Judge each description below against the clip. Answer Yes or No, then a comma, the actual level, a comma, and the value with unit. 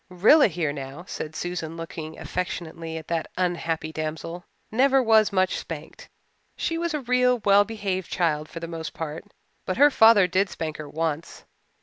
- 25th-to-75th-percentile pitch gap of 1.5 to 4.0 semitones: No, average, 4.7 semitones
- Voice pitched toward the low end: No, medium, 175 Hz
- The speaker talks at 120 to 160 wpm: No, average, 170 wpm